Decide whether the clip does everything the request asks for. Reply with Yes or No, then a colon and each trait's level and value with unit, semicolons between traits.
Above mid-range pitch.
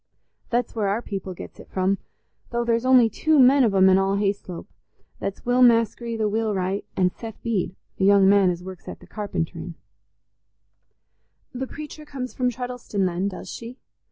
Yes: high, 210 Hz